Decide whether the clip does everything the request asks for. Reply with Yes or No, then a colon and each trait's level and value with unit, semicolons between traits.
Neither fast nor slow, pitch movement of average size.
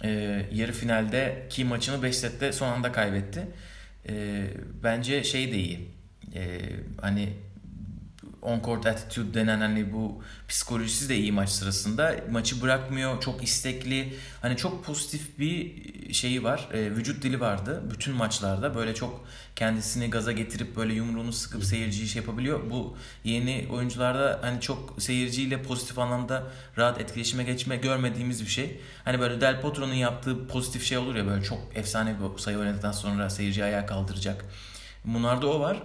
No: fast, 150 wpm; average, 3.5 semitones